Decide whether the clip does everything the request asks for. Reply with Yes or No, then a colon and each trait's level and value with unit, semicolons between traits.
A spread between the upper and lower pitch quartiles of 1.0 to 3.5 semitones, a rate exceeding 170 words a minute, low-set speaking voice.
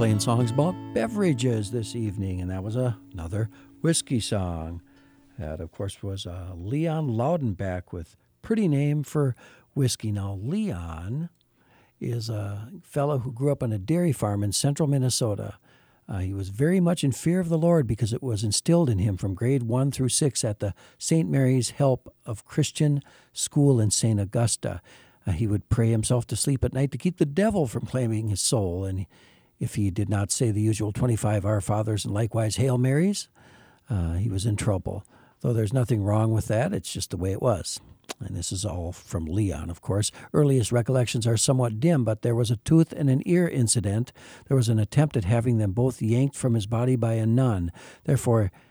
No: average, 4.8 semitones; average, 195 wpm; low, 120 Hz